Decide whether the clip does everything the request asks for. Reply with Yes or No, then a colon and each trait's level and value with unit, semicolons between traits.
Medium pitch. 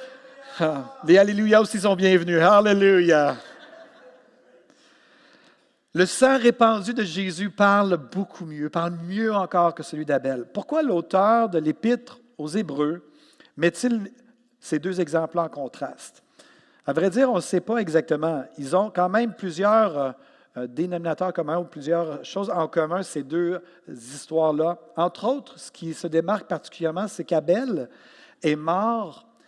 Yes: medium, 180 Hz